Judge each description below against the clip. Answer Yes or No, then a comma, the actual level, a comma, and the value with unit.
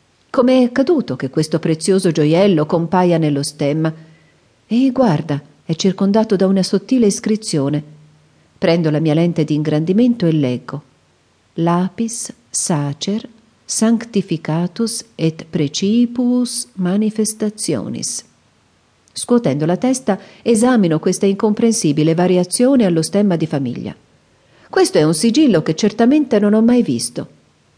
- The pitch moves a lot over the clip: Yes, wide, 6.3 semitones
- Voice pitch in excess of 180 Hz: Yes, high, 190 Hz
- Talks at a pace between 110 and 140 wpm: Yes, slow, 115 wpm